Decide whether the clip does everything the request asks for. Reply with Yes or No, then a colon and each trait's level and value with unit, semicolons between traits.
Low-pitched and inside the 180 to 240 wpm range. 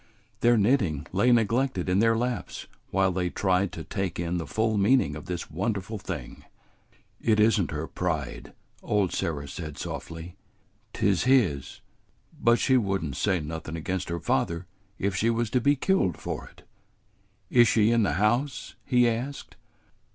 No: very low, 95 Hz; average, 165 wpm